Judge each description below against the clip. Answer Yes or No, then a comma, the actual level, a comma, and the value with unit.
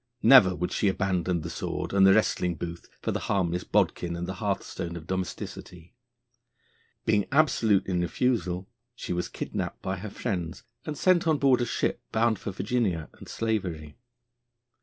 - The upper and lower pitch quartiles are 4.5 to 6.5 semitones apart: No, average, 4.1 semitones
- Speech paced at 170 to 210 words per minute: No, average, 160 wpm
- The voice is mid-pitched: No, very low, 95 Hz